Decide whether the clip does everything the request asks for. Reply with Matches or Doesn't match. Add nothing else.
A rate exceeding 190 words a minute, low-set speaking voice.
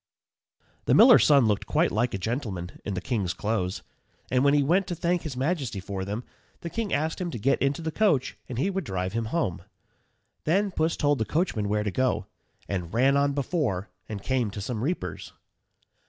Matches